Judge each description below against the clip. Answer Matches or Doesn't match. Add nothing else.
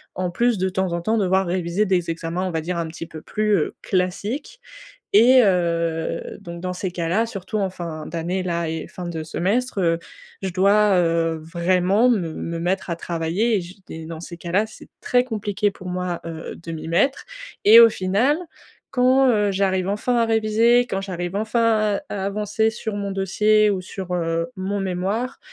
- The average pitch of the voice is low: Doesn't match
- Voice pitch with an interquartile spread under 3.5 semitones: Doesn't match